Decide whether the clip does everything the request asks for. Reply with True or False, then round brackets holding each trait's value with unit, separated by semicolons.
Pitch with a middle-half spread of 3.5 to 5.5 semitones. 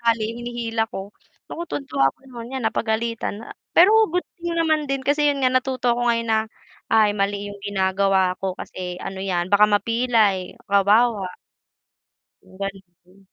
True (3.8 semitones)